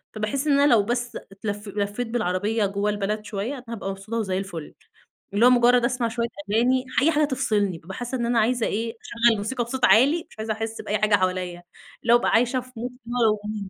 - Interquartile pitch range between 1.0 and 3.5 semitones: Yes, average, 3.1 semitones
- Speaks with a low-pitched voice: No, high, 225 Hz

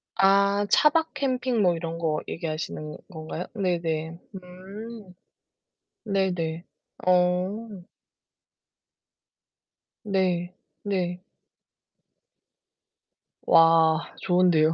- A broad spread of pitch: No, average, 3.2 semitones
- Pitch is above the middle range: No, medium, 180 Hz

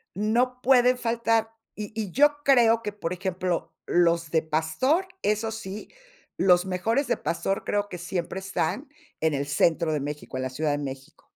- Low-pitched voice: No, high, 195 Hz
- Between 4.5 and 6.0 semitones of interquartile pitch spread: Yes, wide, 5.6 semitones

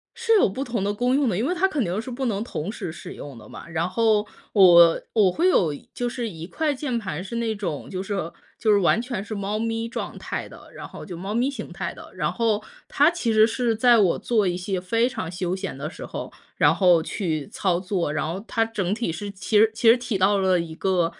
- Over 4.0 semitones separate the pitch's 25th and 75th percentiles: Yes, average, 4.5 semitones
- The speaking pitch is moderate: No, high, 205 Hz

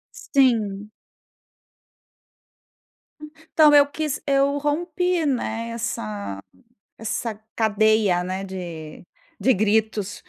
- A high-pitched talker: Yes, high, 220 Hz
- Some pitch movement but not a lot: No, wide, 6.4 semitones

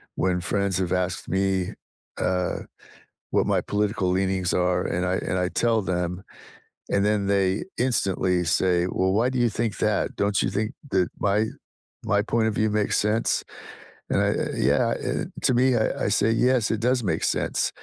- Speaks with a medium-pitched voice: No, low, 100 Hz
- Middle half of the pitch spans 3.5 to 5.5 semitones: No, average, 3.0 semitones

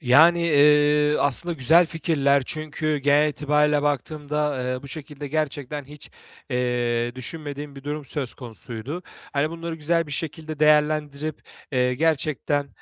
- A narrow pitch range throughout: Yes, narrow, 1.9 semitones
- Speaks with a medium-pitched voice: Yes, medium, 150 Hz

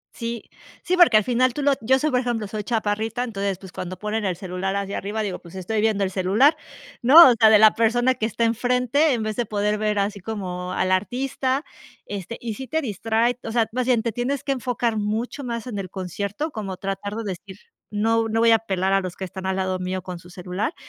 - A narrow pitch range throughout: No, average, 3.8 semitones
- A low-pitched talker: No, high, 215 Hz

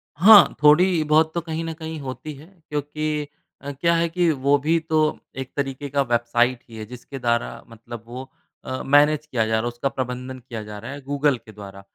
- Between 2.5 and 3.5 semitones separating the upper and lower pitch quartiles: No, average, 4.2 semitones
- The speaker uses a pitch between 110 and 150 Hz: Yes, medium, 140 Hz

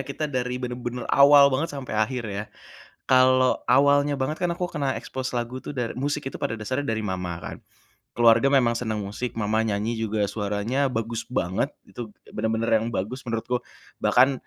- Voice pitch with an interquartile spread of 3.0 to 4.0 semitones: Yes, average, 3.3 semitones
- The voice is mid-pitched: No, low, 125 Hz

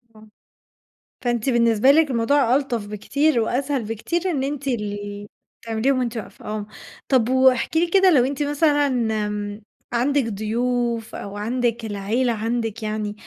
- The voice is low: No, high, 235 Hz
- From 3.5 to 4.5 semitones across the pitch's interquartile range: Yes, average, 4.0 semitones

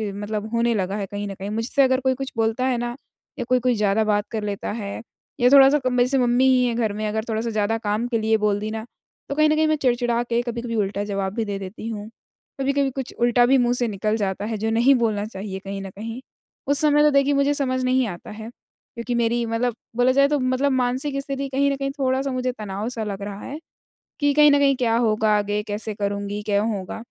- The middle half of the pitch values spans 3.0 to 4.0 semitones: Yes, average, 3.7 semitones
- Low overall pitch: No, high, 235 Hz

